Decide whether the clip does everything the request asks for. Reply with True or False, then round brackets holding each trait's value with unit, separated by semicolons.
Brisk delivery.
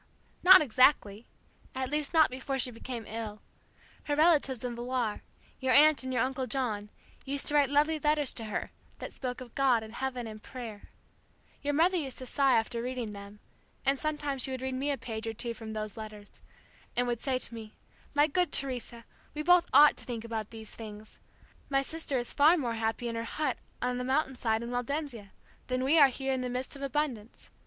True (210 wpm)